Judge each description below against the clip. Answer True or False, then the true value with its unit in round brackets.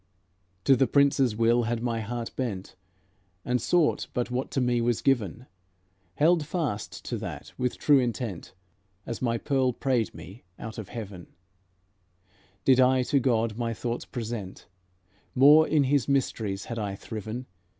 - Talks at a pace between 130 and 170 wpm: True (150 wpm)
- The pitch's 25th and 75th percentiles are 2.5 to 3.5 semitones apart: True (3.0 semitones)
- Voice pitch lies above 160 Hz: False (120 Hz)